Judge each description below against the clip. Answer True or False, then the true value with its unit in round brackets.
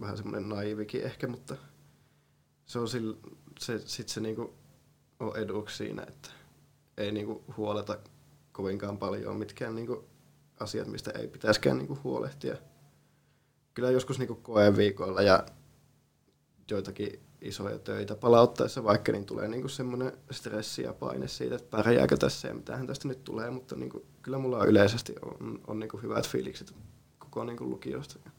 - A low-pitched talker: True (110 Hz)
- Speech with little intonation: False (3.4 semitones)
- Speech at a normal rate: True (140 wpm)